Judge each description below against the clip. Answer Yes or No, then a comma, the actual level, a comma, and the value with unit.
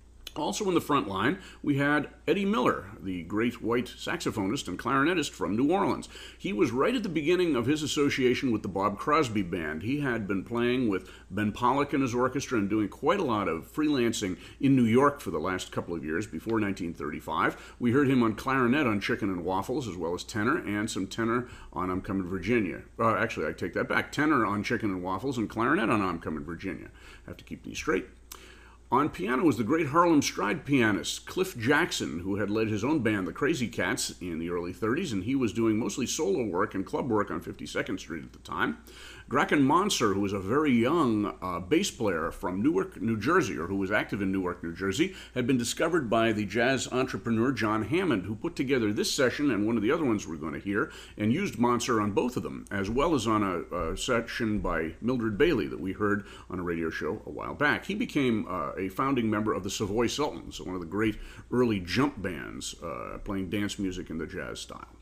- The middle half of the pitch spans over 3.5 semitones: Yes, average, 4.4 semitones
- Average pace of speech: No, fast, 220 wpm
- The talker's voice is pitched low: Yes, low, 110 Hz